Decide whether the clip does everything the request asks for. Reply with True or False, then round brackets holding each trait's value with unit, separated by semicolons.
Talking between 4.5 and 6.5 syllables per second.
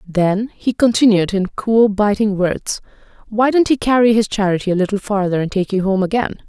True (5.2 syllables/s)